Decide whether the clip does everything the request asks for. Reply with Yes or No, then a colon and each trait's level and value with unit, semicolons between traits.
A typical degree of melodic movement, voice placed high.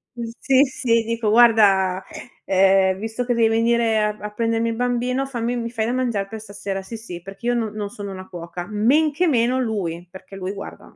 Yes: average, 3.4 semitones; high, 225 Hz